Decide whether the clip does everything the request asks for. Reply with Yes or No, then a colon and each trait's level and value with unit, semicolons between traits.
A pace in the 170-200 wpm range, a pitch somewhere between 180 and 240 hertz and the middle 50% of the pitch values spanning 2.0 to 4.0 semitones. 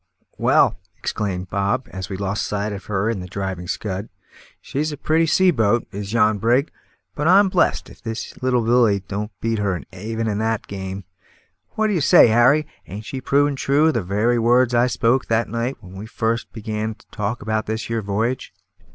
No: average, 190 wpm; low, 110 Hz; average, 3.7 semitones